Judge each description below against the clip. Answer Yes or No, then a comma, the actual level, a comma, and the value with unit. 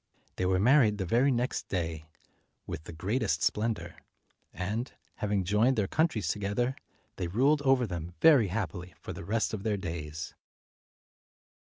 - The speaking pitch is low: Yes, low, 105 Hz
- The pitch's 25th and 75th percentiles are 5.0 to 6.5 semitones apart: Yes, wide, 5.4 semitones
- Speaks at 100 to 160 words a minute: Yes, average, 150 wpm